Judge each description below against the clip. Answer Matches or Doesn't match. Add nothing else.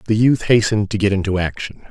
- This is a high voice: Doesn't match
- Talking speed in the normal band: Doesn't match